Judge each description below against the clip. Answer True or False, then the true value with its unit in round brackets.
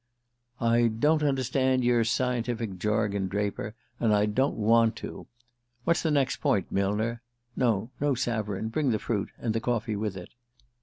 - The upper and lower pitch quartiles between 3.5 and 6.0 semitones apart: False (3.1 semitones)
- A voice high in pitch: False (115 Hz)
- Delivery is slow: False (155 wpm)